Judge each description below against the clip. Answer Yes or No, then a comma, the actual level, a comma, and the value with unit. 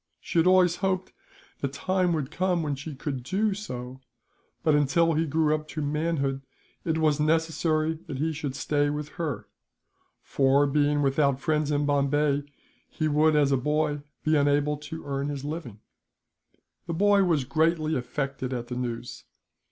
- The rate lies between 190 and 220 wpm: No, average, 165 wpm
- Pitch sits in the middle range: Yes, medium, 150 Hz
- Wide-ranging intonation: No, narrow, 2.5 semitones